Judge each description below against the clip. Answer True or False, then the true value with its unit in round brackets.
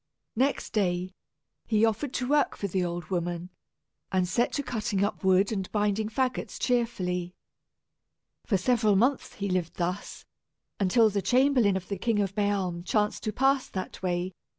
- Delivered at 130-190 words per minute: True (160 wpm)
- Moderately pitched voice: False (200 Hz)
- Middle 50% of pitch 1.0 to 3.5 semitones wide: False (4.1 semitones)